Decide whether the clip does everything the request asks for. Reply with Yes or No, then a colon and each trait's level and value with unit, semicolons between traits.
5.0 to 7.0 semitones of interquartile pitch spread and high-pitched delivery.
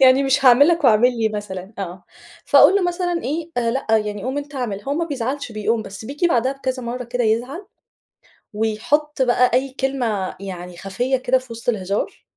No: average, 4.2 semitones; high, 245 Hz